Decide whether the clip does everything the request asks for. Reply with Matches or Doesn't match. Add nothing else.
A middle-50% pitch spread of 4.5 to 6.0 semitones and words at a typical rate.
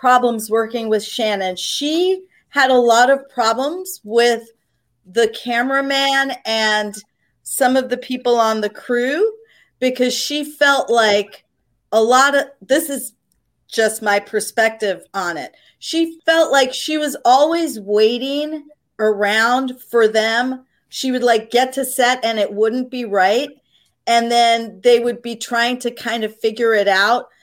Doesn't match